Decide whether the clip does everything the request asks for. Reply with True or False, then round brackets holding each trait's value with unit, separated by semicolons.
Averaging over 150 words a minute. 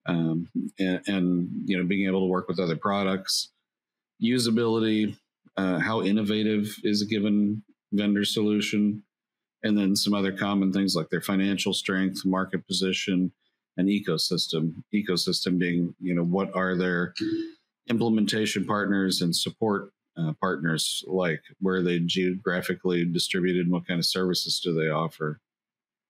False (145 wpm)